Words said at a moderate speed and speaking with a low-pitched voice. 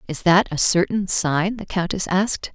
No: average, 190 wpm; medium, 185 Hz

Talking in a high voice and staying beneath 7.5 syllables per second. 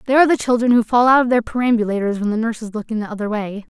No: high, 225 Hz; 7.7 syllables/s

